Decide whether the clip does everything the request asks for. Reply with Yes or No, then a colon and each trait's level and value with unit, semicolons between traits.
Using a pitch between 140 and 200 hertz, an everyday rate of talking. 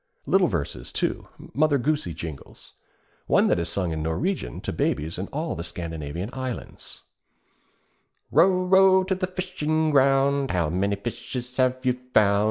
No: low, 125 Hz; average, 150 wpm